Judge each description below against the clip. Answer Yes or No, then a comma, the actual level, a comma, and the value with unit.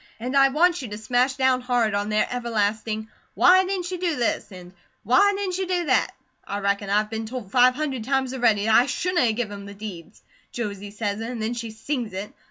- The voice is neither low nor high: No, high, 235 Hz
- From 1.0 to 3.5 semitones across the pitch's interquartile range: No, average, 4.3 semitones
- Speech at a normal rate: No, fast, 230 wpm